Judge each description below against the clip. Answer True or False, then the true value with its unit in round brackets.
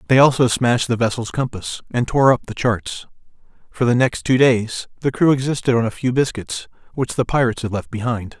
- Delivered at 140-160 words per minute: False (205 wpm)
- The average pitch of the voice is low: True (120 Hz)